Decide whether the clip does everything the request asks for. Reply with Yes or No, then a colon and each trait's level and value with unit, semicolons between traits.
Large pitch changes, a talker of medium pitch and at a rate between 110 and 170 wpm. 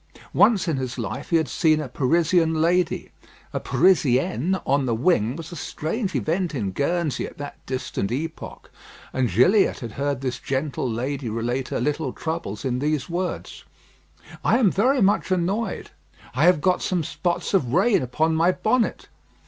Yes: wide, 5.7 semitones; medium, 155 Hz; average, 165 wpm